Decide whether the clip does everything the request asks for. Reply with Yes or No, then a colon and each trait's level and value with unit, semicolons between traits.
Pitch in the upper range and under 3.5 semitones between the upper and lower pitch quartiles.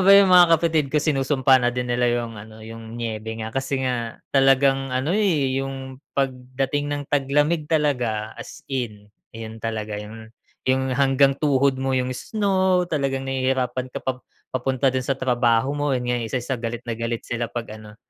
No: low, 130 Hz; average, 2.8 semitones